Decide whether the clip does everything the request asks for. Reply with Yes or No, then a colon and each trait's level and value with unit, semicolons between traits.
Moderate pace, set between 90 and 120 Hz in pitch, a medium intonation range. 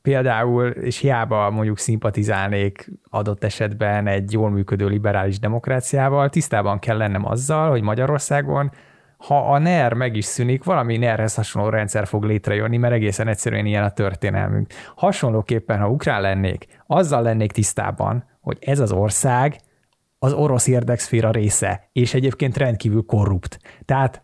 Yes: average, 140 wpm; low, 115 Hz; average, 4.0 semitones